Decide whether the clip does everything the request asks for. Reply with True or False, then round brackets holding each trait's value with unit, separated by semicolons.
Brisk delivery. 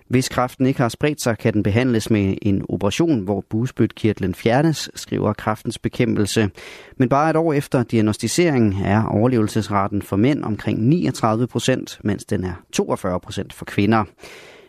False (155 wpm)